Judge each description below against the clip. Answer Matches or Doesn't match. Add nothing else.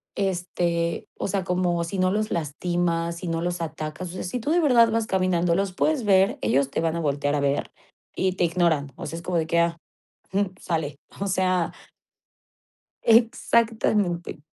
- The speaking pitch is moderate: Matches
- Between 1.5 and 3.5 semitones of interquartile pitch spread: Matches